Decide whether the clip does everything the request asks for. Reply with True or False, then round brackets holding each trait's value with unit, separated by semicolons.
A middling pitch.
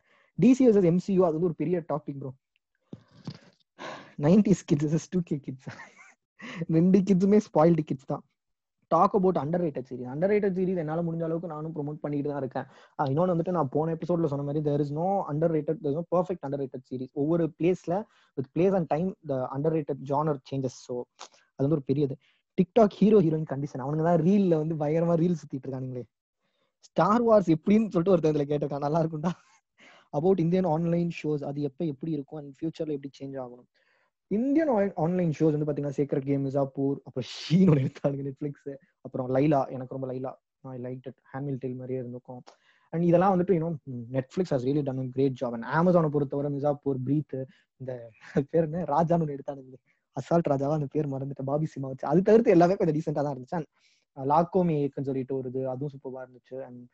True (150 Hz)